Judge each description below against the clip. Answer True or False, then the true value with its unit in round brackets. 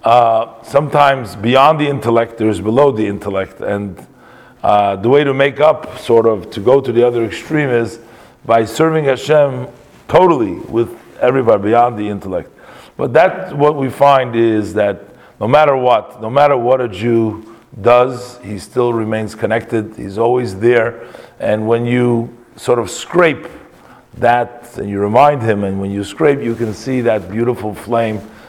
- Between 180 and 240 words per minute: False (165 wpm)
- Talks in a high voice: False (115 Hz)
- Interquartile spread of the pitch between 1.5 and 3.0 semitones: True (2.7 semitones)